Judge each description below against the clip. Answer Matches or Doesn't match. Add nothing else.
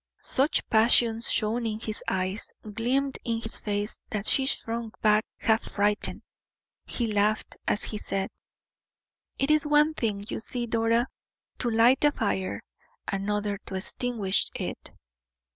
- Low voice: Doesn't match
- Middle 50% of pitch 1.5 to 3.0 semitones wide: Matches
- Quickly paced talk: Doesn't match